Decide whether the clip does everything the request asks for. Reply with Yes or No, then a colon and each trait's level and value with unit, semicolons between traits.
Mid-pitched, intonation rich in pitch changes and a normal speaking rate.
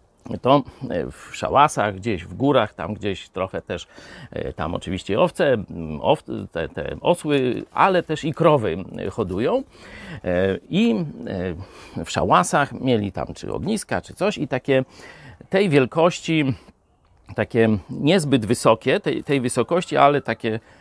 No: low, 130 Hz; wide, 6.5 semitones; average, 125 wpm